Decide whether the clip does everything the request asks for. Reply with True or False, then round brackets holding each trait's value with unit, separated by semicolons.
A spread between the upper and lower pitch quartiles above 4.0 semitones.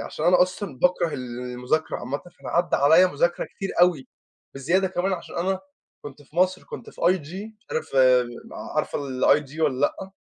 True (5.1 semitones)